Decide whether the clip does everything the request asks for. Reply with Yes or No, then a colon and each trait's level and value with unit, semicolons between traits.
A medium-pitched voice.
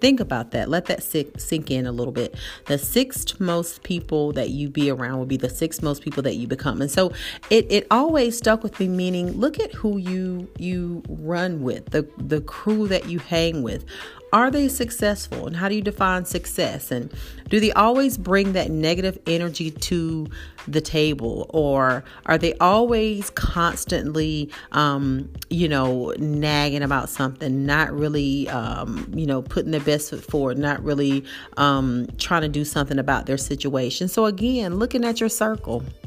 Yes: medium, 160 Hz